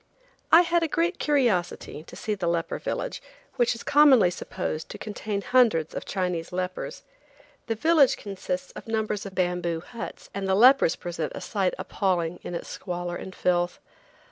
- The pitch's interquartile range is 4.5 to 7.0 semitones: Yes, average, 5.1 semitones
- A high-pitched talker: Yes, high, 195 Hz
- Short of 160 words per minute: No, average, 170 wpm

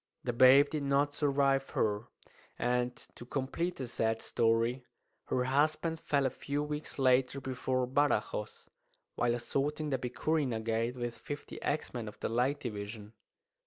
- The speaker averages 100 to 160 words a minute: Yes, average, 145 wpm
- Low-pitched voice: Yes, low, 130 Hz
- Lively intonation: No, average, 3.2 semitones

